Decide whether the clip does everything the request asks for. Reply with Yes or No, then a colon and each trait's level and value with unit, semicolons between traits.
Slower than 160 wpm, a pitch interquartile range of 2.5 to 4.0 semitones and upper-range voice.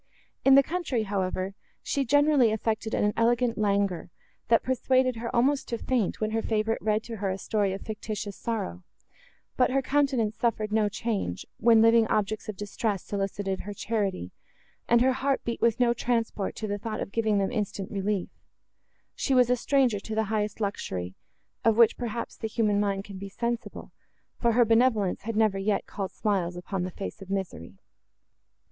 No: average, 180 wpm; average, 2.9 semitones; high, 220 Hz